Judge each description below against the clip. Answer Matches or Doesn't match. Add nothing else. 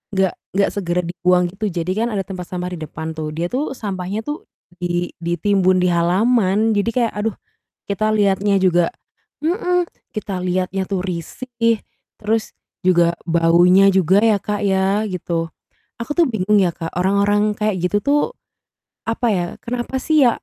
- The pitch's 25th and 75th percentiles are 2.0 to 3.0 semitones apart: Doesn't match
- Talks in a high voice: Matches